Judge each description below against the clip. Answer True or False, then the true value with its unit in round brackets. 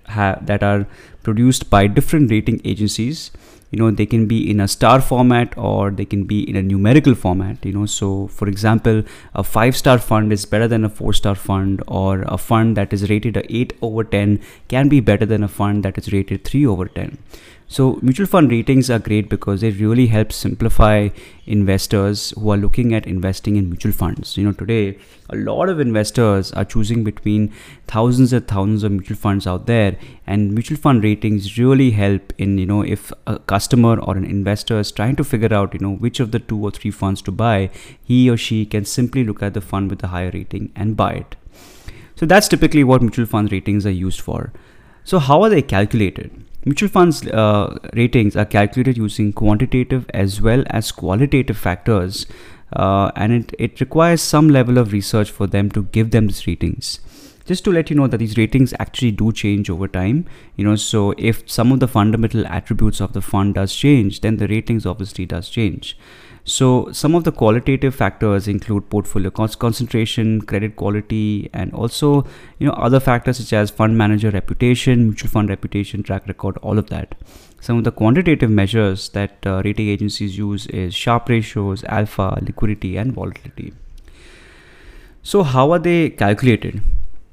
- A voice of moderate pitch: False (105 Hz)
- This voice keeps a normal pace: True (190 wpm)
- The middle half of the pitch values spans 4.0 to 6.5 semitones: False (3.1 semitones)